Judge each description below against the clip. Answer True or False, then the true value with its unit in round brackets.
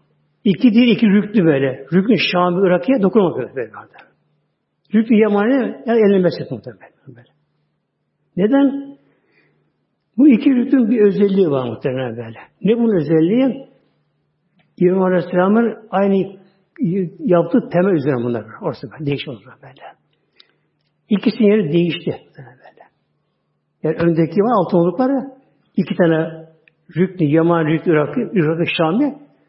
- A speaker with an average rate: True (120 wpm)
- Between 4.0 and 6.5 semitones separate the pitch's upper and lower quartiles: True (5.6 semitones)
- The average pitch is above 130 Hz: True (185 Hz)